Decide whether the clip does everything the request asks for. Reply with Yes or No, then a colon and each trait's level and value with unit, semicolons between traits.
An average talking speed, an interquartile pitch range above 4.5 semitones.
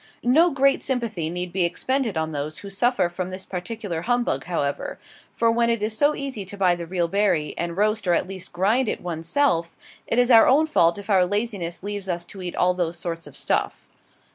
No: fast, 215 wpm; average, 5.1 semitones